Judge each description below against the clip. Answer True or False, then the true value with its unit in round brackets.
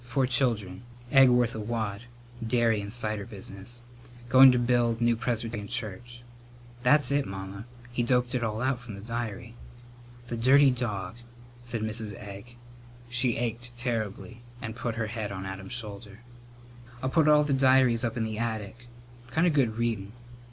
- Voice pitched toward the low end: True (120 Hz)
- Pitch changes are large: False (2.4 semitones)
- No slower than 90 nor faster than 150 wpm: False (165 wpm)